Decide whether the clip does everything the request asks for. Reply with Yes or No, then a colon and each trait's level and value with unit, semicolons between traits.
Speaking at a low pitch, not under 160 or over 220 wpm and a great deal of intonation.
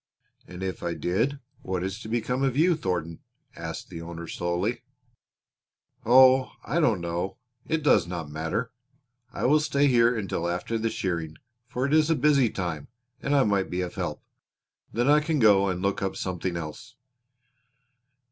Yes: low, 105 Hz; average, 170 wpm; wide, 6.9 semitones